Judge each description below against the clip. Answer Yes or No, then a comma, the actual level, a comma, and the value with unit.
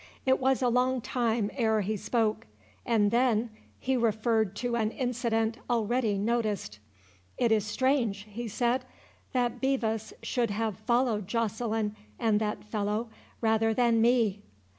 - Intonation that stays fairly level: Yes, narrow, 2.2 semitones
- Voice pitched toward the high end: Yes, high, 225 Hz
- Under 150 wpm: Yes, average, 140 wpm